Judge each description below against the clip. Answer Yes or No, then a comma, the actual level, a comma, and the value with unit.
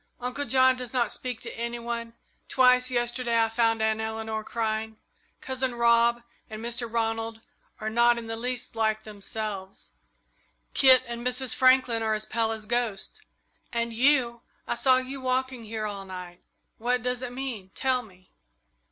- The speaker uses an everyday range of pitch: No, narrow, 2.2 semitones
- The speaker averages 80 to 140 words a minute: No, average, 160 wpm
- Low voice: No, high, 235 Hz